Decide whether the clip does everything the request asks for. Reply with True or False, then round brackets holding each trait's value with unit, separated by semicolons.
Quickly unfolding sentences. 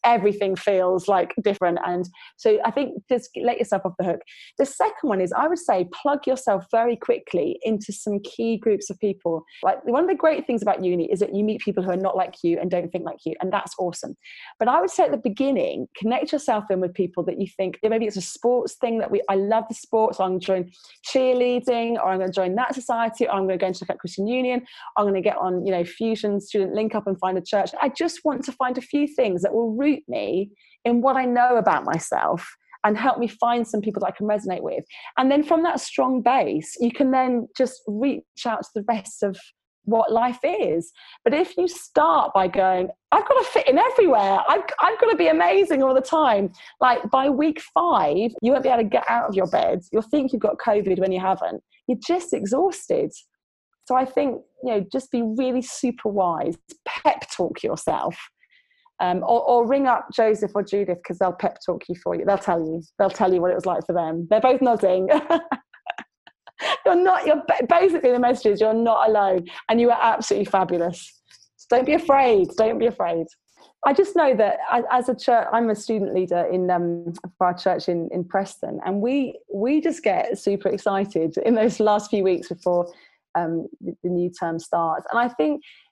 True (225 wpm)